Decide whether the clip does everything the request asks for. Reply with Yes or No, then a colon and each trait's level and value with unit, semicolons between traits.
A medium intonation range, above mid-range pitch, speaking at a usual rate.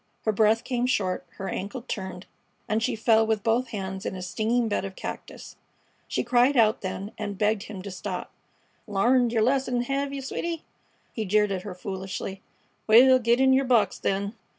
Yes: average, 3.9 semitones; high, 220 Hz; average, 185 wpm